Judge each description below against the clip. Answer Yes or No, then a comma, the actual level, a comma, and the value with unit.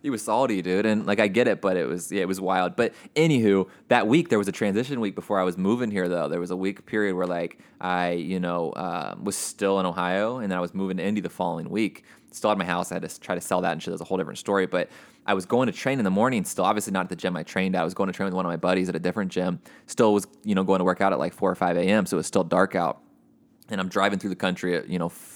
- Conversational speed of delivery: No, fast, 320 wpm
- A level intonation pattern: Yes, narrow, 1.3 semitones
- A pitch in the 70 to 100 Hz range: Yes, very low, 95 Hz